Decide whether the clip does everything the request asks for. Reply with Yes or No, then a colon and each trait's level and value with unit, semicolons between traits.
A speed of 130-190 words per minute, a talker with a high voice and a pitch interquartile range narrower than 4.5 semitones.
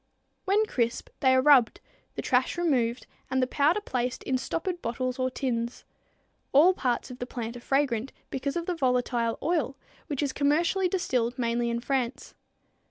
Yes: average, 165 wpm; very high, 260 Hz; average, 3.5 semitones